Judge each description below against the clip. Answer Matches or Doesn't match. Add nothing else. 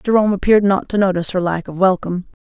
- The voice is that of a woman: Matches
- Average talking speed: Doesn't match